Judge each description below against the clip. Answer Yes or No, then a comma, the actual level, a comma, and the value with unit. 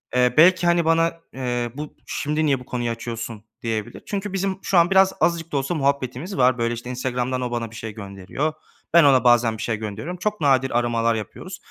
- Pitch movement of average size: No, wide, 5.7 semitones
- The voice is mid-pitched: No, low, 130 Hz